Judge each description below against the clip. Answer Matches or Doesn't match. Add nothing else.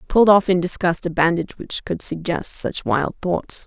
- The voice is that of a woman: Matches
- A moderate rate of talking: Doesn't match